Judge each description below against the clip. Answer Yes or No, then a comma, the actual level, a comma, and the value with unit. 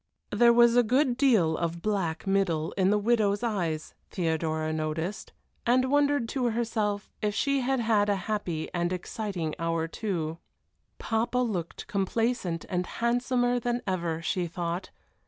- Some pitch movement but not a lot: No, wide, 5.9 semitones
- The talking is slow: No, average, 145 wpm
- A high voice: Yes, high, 205 Hz